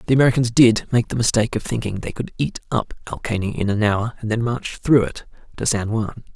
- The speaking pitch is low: Yes, low, 115 Hz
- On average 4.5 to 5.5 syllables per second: No, 6.0 syllables/s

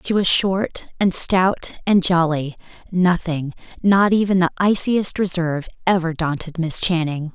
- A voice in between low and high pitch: Yes, medium, 175 Hz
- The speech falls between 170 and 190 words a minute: No, average, 140 wpm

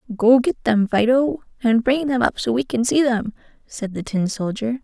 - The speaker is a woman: Yes, female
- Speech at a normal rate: No, fast, 210 wpm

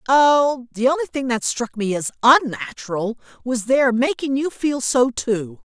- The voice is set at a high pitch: Yes, very high, 250 Hz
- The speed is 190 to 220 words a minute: No, average, 170 wpm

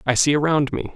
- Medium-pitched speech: Yes, medium, 145 Hz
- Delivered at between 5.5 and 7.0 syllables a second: Yes, 6.0 syllables/s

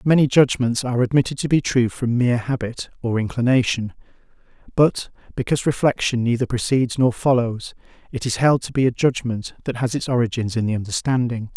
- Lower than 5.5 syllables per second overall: No, 6.0 syllables/s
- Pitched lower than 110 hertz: No, low, 125 Hz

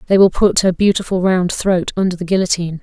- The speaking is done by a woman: Yes, female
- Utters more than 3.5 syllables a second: Yes, 6.2 syllables/s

